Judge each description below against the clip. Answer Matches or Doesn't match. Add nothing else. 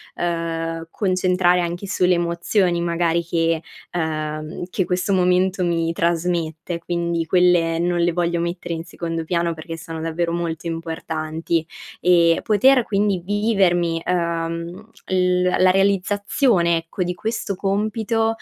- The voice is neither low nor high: Matches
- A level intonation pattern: Matches